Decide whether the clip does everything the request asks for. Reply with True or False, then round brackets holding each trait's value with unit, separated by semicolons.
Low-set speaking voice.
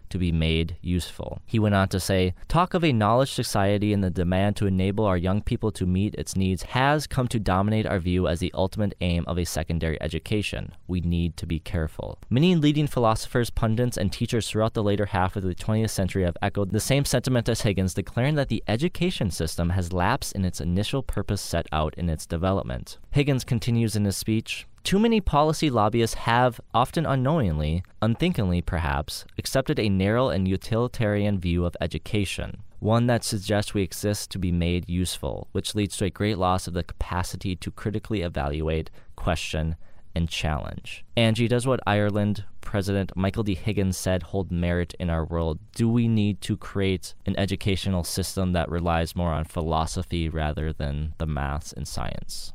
True (95 Hz)